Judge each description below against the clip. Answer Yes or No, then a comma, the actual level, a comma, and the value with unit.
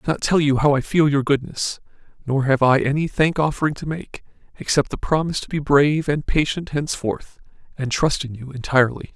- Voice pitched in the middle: Yes, medium, 145 Hz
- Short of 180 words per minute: No, fast, 205 wpm